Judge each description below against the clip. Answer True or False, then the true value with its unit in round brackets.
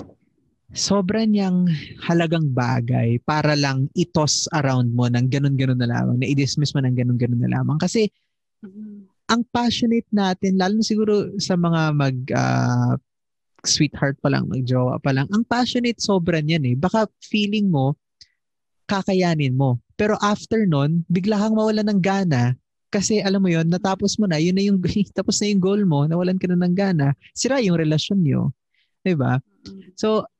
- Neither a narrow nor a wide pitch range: False (6.9 semitones)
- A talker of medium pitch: True (175 Hz)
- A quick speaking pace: True (160 wpm)